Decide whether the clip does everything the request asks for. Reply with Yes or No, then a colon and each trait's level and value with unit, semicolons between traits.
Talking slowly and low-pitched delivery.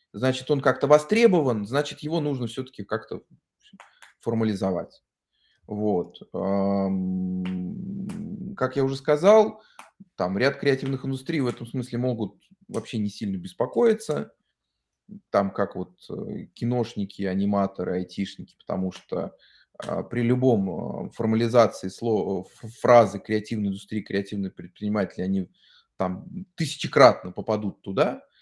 Yes: slow, 105 wpm; low, 120 Hz